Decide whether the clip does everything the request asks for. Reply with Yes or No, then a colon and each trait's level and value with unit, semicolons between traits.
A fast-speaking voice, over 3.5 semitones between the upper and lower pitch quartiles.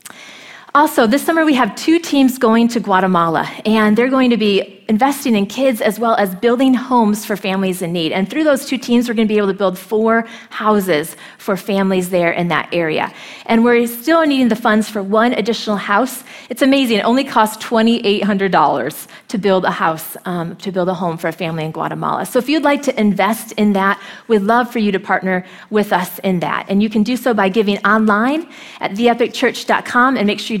Yes: fast, 220 wpm; average, 4.0 semitones